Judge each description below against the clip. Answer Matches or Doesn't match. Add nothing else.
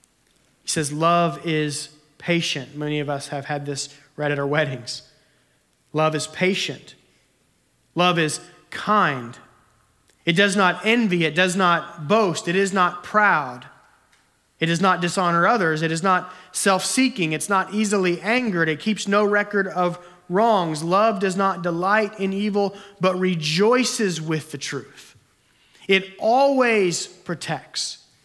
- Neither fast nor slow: Matches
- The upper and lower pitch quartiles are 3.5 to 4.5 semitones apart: Matches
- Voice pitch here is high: Doesn't match